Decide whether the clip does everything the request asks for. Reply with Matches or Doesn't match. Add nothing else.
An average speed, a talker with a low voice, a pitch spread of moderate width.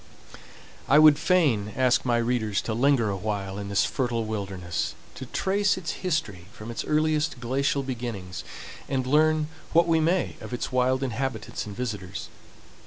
Doesn't match